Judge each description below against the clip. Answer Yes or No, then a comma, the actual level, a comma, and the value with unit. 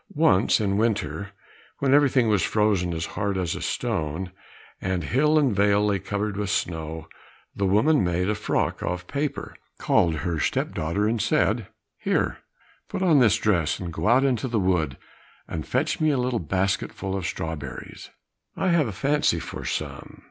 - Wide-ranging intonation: Yes, wide, 6.1 semitones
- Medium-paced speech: Yes, average, 170 wpm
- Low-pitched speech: Yes, low, 100 Hz